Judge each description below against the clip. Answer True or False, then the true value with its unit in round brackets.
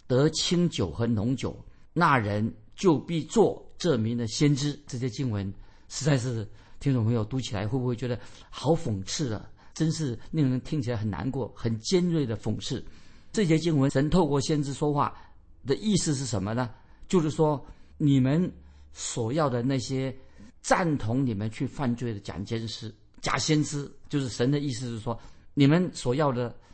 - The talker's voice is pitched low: True (130 Hz)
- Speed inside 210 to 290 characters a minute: True (245 characters per minute)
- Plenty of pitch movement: False (5.0 semitones)